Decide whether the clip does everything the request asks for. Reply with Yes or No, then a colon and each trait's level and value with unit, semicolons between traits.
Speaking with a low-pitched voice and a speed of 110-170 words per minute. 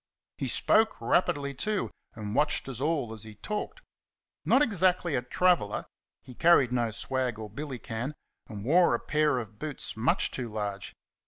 Yes: low, 130 Hz; average, 160 wpm